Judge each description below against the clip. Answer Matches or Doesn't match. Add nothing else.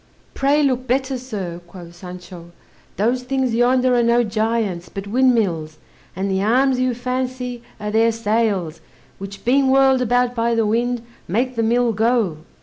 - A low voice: Doesn't match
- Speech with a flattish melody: Doesn't match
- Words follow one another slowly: Doesn't match